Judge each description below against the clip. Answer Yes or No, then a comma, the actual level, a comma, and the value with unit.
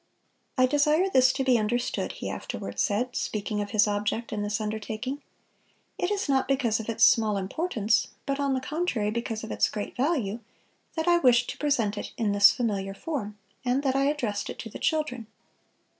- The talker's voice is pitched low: No, high, 240 Hz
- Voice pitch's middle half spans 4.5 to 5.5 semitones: Yes, average, 4.8 semitones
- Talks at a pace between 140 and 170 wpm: No, average, 190 wpm